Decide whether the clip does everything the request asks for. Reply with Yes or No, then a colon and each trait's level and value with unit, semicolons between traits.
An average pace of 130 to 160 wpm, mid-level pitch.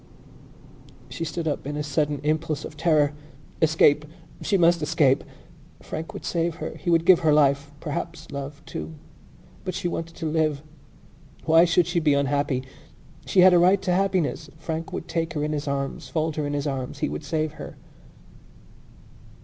No: average, 175 wpm; medium, 155 Hz